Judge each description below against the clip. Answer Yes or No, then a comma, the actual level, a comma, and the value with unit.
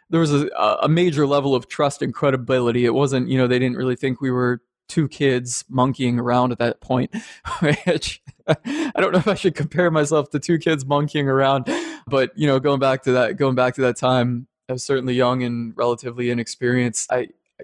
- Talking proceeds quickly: Yes, fast, 210 wpm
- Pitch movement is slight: No, average, 3.4 semitones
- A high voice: No, low, 135 Hz